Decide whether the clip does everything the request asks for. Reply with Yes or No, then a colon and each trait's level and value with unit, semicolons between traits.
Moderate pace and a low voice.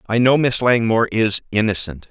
Yes: average, 170 wpm; low, 110 Hz